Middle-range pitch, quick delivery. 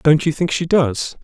Yes: medium, 155 Hz; fast, 240 wpm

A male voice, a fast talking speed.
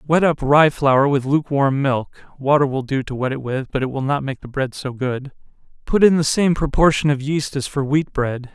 Yes: male; fast, 240 wpm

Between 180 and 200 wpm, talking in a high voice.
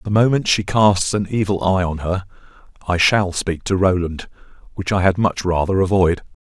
No: average, 185 wpm; very low, 95 Hz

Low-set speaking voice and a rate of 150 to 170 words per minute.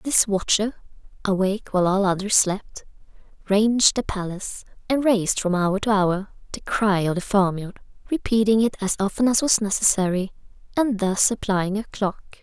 No: high, 205 Hz; average, 160 wpm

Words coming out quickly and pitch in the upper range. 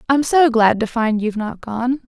Yes: fast, 225 wpm; high, 235 Hz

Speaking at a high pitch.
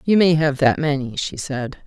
No: medium, 145 Hz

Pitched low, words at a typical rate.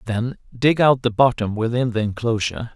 Yes: low, 115 Hz; average, 175 wpm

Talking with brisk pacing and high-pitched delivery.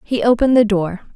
Yes: fast, 210 wpm; high, 220 Hz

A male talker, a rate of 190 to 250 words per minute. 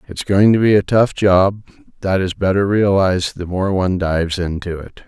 Yes: male; average, 200 wpm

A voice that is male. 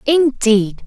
No: female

